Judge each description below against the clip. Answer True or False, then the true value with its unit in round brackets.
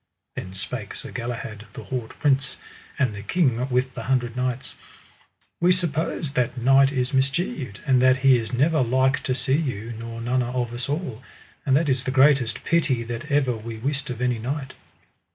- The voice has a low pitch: True (130 Hz)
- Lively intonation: False (2.5 semitones)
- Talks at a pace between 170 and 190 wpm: True (185 wpm)